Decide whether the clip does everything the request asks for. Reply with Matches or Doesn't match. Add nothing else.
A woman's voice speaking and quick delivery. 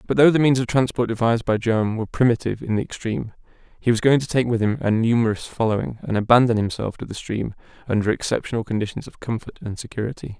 Doesn't match